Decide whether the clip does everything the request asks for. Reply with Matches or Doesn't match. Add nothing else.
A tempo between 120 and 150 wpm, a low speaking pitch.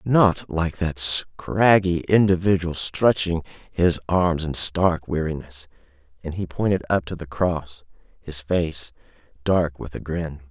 Matches